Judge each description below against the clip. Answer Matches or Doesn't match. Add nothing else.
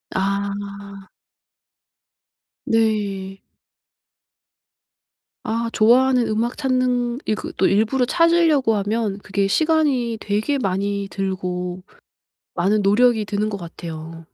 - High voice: Matches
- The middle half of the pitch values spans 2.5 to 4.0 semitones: Matches